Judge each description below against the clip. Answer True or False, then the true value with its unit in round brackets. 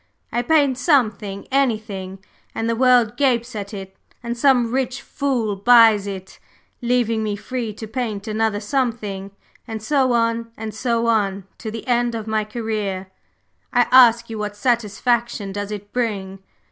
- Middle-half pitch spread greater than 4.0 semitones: False (2.8 semitones)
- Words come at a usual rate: True (155 wpm)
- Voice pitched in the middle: False (225 Hz)